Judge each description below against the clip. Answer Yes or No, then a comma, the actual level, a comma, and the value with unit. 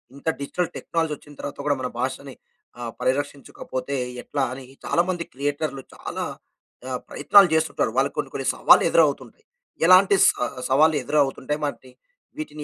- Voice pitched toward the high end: No, medium, 145 Hz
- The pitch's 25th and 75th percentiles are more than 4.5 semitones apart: No, average, 3.2 semitones